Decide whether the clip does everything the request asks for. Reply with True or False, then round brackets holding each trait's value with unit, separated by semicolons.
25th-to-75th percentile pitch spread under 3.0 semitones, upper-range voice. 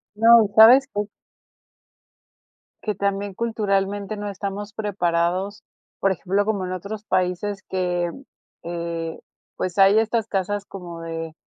True (2.6 semitones; 195 Hz)